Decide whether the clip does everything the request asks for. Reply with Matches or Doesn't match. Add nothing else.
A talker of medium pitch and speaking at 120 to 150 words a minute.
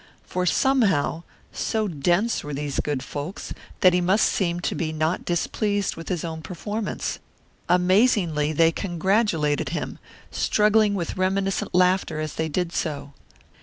Matches